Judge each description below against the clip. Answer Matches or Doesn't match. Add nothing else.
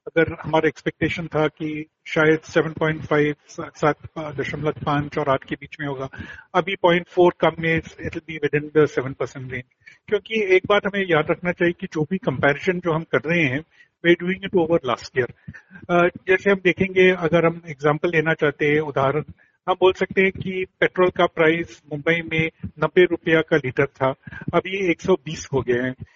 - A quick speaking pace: Doesn't match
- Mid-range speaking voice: Matches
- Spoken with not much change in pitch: Doesn't match